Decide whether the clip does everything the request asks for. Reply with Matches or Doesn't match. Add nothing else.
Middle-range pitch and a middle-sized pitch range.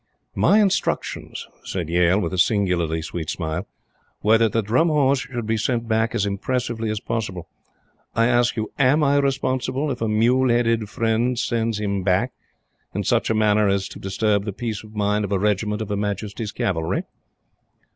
Doesn't match